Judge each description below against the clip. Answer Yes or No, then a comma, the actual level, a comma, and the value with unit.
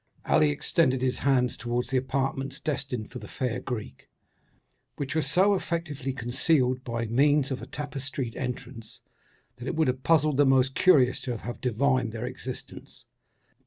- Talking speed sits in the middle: Yes, average, 160 wpm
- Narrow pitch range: Yes, narrow, 2.3 semitones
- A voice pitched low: Yes, low, 130 Hz